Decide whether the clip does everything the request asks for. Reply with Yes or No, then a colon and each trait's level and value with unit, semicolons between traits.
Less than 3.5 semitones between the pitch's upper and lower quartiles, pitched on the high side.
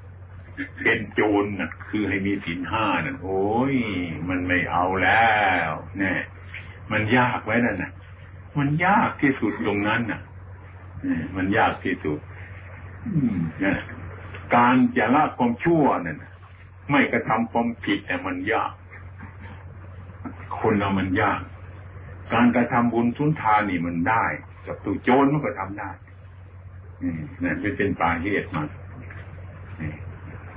No: narrow, 2.5 semitones; very low, 95 Hz